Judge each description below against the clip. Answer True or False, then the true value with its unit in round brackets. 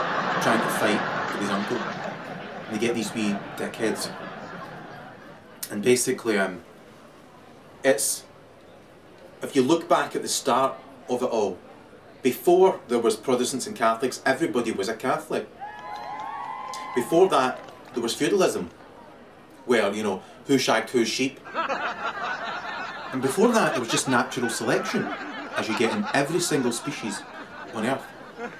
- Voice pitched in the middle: False (125 Hz)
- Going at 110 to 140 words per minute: True (135 wpm)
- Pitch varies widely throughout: False (2.9 semitones)